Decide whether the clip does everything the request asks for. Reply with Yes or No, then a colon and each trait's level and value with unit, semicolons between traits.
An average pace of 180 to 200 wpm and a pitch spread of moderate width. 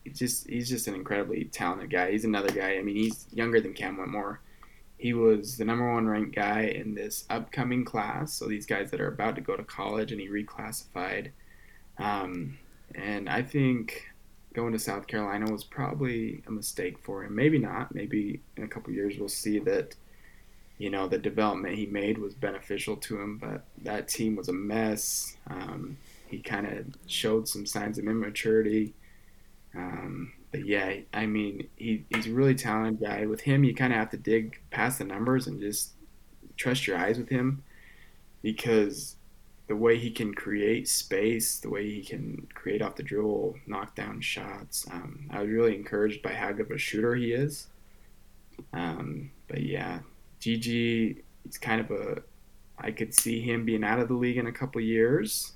No: average, 185 wpm; narrow, 2.3 semitones